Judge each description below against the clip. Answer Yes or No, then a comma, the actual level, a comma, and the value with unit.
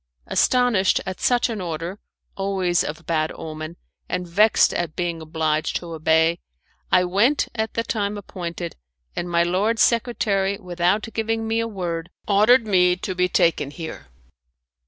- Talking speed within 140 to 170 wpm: Yes, average, 150 wpm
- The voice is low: No, medium, 180 Hz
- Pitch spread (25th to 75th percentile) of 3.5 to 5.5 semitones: Yes, average, 4.0 semitones